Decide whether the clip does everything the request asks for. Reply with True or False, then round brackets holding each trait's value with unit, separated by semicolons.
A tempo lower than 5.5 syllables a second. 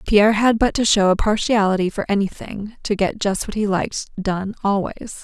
True (5.2 syllables/s)